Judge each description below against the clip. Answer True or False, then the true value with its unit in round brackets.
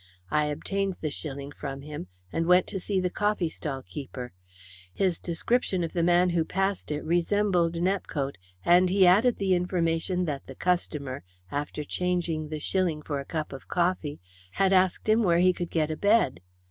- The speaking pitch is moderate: True (175 Hz)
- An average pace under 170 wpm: False (175 wpm)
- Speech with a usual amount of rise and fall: True (3.5 semitones)